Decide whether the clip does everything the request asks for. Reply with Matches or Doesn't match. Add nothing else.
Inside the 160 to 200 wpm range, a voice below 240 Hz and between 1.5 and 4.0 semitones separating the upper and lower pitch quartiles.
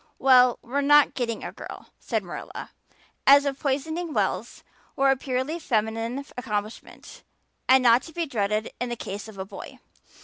Doesn't match